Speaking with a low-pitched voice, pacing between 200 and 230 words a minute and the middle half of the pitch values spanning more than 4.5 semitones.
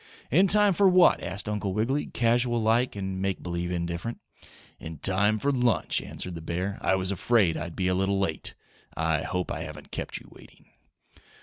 No: very low, 95 Hz; average, 185 wpm; average, 5.0 semitones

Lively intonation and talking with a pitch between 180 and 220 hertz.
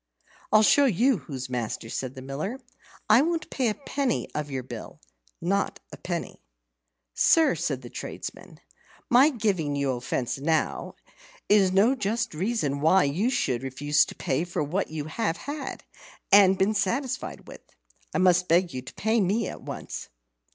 Yes: wide, 8.0 semitones; medium, 185 Hz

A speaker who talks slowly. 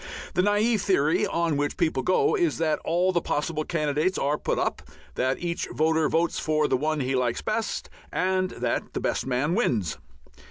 No: average, 185 wpm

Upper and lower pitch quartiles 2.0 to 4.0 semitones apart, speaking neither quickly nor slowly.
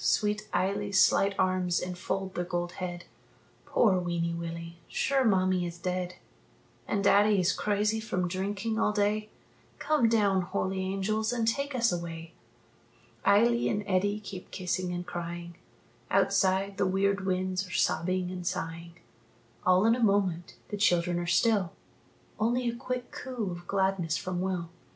Yes: average, 2.9 semitones; average, 150 wpm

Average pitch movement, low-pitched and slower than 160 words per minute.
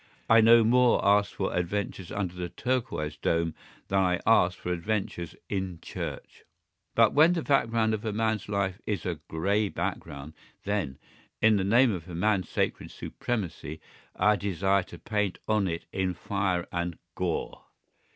Yes: average, 3.6 semitones; low, 100 Hz; average, 150 wpm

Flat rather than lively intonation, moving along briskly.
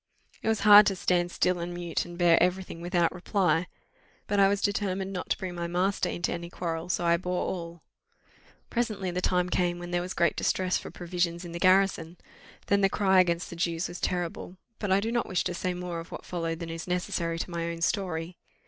Yes: narrow, 1.7 semitones; fast, 225 wpm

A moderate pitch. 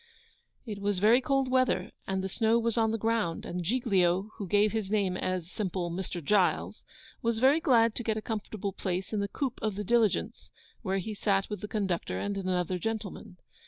No: high, 205 Hz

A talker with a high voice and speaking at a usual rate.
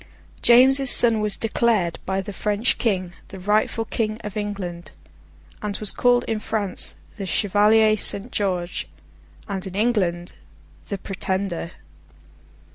No: high, 205 Hz; slow, 125 wpm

